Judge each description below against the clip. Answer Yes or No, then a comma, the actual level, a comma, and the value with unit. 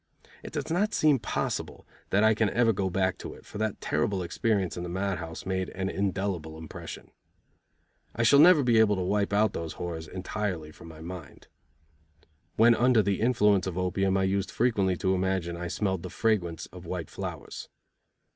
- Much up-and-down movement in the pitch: No, average, 3.4 semitones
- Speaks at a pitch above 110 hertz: No, very low, 95 Hz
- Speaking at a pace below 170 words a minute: No, average, 185 wpm